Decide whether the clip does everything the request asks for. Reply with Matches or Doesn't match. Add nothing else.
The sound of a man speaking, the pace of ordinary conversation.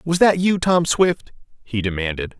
Matches